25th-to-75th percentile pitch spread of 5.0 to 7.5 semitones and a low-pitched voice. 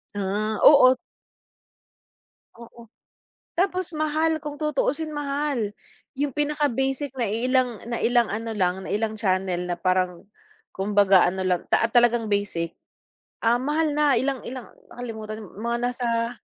No: wide, 5.5 semitones; high, 235 Hz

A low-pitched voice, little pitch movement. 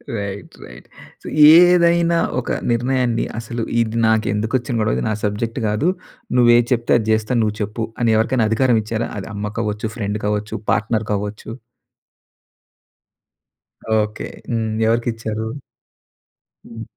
Yes: low, 110 Hz; narrow, 2.0 semitones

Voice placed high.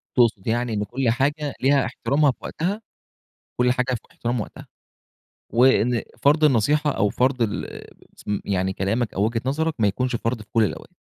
No: low, 125 Hz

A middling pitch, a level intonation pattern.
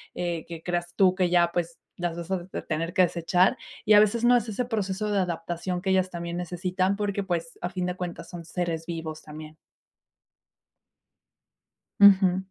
Yes: medium, 180 Hz; narrow, 2.0 semitones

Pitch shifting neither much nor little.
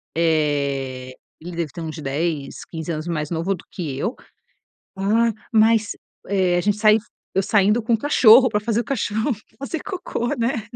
No: wide, 6.1 semitones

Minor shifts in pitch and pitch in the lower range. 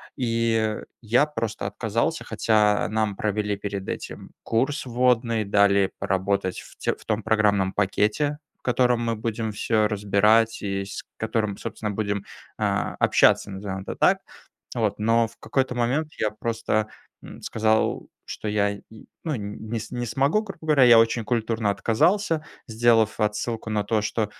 Yes: narrow, 2.3 semitones; low, 110 Hz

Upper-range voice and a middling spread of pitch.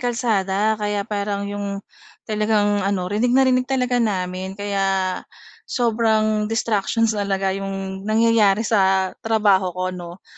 No: high, 205 Hz; narrow, 2.3 semitones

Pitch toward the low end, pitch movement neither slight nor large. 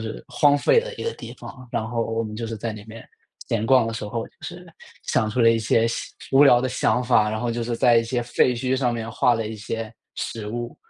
No: low, 115 Hz; narrow, 1.9 semitones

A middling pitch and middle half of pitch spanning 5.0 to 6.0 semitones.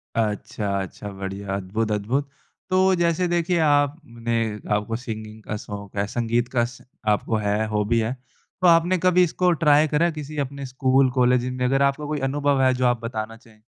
No: low, 125 Hz; average, 5.3 semitones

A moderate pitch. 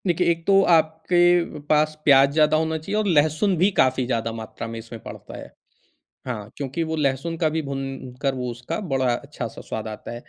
Yes: medium, 145 Hz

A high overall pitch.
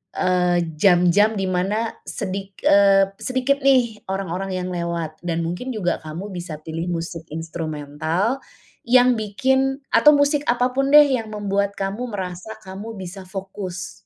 Yes: high, 195 Hz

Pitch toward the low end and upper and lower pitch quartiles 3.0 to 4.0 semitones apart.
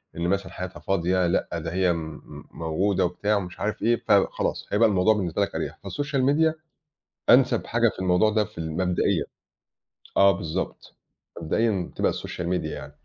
Yes: very low, 95 Hz; average, 3.6 semitones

